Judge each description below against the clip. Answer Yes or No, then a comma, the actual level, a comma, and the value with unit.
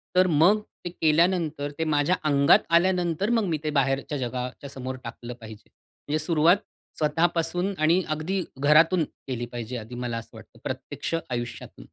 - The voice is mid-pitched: Yes, medium, 155 Hz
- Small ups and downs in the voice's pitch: No, average, 5.0 semitones